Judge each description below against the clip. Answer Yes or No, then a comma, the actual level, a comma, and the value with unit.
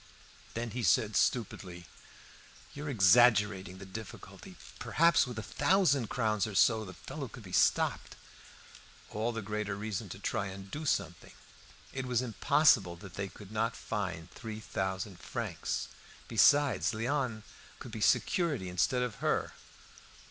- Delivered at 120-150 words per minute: Yes, average, 145 wpm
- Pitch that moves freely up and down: No, average, 4.3 semitones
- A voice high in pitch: No, low, 110 Hz